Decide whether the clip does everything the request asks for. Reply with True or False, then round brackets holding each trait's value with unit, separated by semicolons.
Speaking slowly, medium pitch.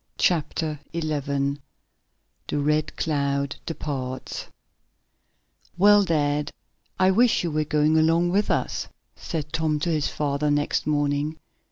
True (120 wpm; 150 Hz)